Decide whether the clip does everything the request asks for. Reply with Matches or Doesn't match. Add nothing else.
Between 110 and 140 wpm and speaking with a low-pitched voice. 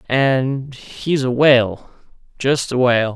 Matches